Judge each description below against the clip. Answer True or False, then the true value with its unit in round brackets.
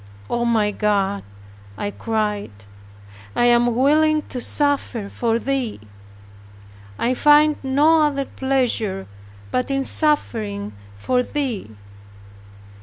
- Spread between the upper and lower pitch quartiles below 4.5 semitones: False (4.8 semitones)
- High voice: True (245 Hz)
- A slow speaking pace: True (105 wpm)